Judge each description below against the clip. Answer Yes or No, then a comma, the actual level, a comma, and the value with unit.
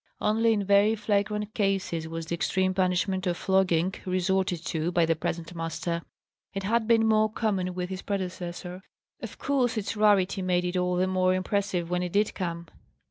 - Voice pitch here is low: No, medium, 185 Hz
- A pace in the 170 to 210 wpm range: Yes, average, 180 wpm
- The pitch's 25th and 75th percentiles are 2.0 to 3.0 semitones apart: Yes, narrow, 2.4 semitones